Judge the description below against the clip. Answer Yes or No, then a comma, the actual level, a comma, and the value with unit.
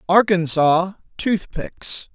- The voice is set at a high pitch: No, medium, 180 Hz